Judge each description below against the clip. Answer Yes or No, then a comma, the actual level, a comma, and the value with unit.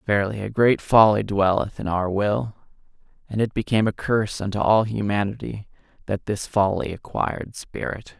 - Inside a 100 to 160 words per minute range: Yes, average, 155 wpm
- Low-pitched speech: Yes, low, 105 Hz